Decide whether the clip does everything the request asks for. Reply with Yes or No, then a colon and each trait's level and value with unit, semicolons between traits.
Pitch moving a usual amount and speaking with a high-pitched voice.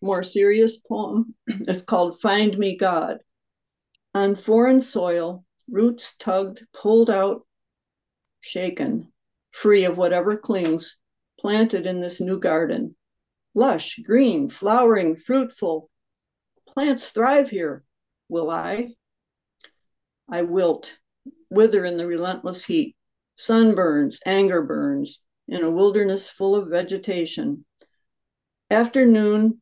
Yes: average, 3.9 semitones; high, 205 Hz